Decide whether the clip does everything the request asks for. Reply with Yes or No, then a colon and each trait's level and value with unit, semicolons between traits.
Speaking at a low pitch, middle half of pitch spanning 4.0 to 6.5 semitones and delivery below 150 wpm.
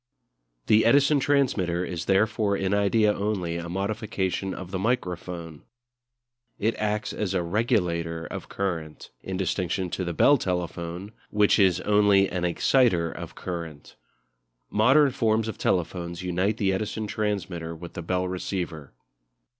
No: very low, 95 Hz; average, 3.5 semitones; average, 140 wpm